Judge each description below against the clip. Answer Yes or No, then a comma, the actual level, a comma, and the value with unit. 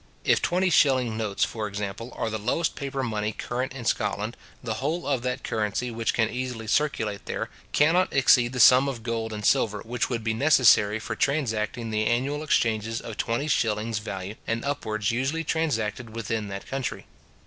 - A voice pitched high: No, low, 115 Hz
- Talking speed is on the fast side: No, average, 180 wpm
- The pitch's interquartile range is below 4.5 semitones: Yes, average, 3.6 semitones